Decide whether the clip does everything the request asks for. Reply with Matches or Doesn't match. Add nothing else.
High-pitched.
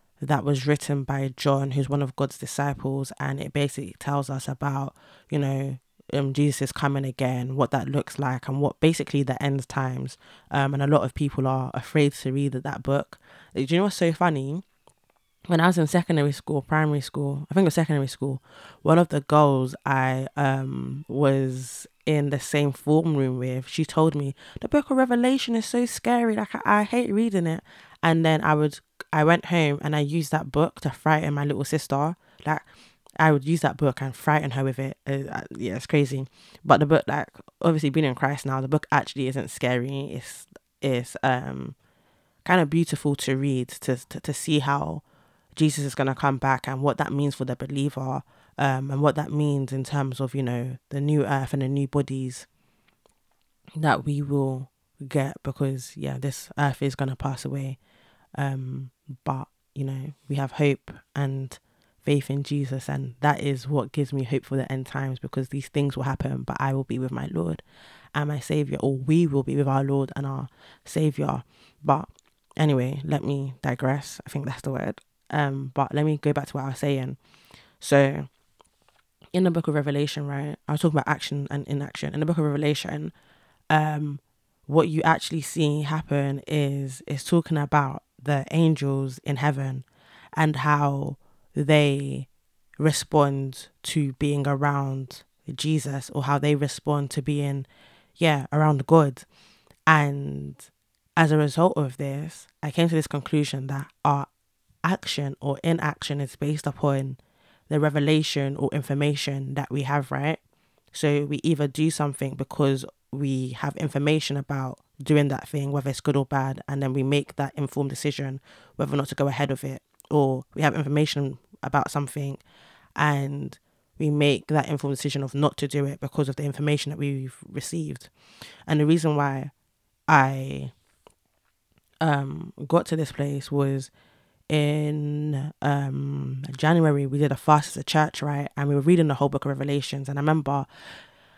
Doesn't match